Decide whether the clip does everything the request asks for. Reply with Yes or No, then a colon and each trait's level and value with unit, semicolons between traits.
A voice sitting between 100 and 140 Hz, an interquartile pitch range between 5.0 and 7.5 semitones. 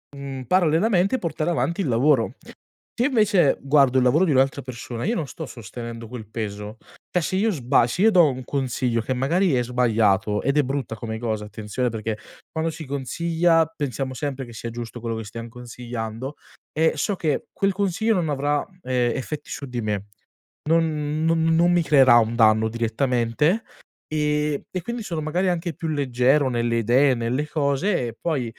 Yes: low, 135 Hz; wide, 5.6 semitones